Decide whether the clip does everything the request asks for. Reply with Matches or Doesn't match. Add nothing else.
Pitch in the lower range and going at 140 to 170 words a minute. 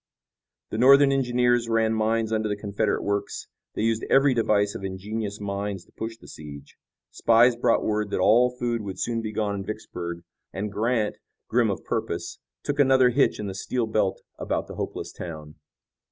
Doesn't match